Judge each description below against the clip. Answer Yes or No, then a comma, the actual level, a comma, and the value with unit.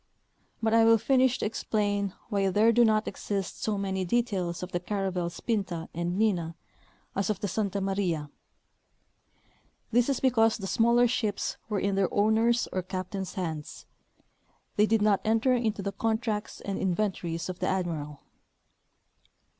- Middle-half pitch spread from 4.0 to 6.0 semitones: No, average, 3.3 semitones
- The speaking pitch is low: No, high, 200 Hz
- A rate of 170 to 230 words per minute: No, average, 160 wpm